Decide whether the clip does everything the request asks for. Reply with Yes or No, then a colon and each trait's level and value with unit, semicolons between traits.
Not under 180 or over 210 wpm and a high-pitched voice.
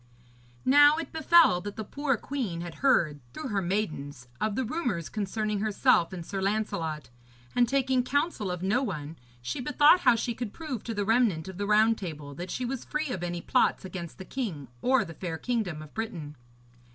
Yes: average, 195 wpm; high, 210 Hz